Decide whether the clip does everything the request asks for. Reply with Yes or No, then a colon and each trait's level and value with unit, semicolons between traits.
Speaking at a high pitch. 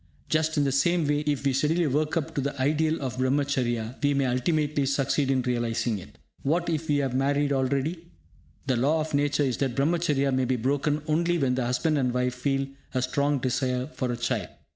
No: medium, 140 Hz